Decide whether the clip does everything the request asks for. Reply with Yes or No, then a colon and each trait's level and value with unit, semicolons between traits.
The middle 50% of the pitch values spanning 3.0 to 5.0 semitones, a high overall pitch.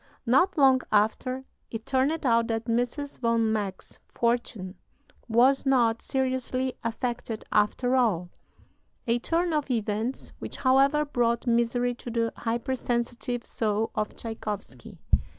No: narrow, 2.5 semitones; high, 240 Hz